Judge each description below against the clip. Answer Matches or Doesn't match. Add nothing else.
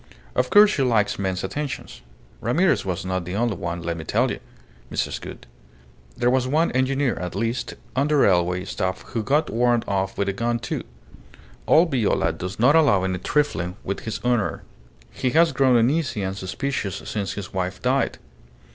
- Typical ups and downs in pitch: Doesn't match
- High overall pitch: Doesn't match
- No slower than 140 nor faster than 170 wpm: Doesn't match